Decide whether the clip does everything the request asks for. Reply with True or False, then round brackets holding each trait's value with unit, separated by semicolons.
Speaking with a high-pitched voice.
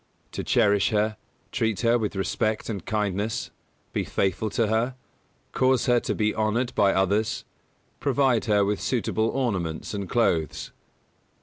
False (110 Hz)